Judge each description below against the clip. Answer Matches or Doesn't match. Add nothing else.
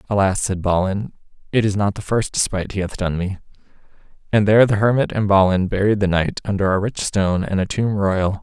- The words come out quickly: Matches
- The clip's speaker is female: Doesn't match